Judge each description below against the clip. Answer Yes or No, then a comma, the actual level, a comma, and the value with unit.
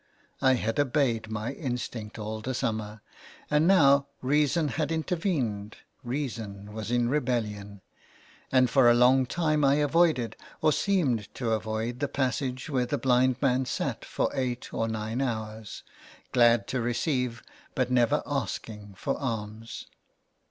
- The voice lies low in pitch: Yes, low, 125 Hz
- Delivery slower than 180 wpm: Yes, average, 140 wpm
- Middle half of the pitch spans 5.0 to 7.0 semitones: No, average, 3.9 semitones